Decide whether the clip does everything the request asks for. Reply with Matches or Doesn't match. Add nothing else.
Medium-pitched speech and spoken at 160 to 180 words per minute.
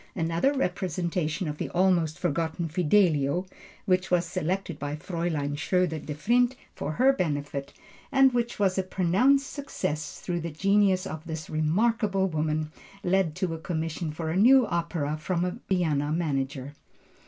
Doesn't match